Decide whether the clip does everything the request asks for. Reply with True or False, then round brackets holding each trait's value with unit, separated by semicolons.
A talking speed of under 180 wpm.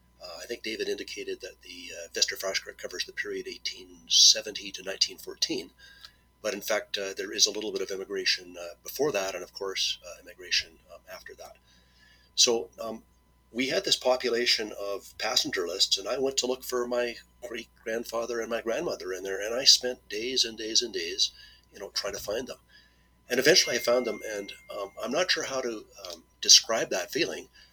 False (195 wpm)